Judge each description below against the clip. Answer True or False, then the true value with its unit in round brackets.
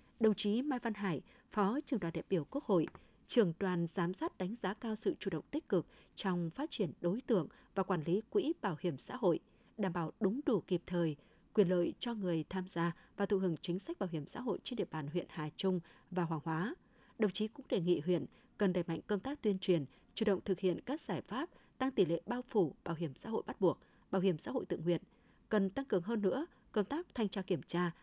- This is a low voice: False (190 Hz)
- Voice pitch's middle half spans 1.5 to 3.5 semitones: False (4.3 semitones)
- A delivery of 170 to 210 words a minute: False (245 wpm)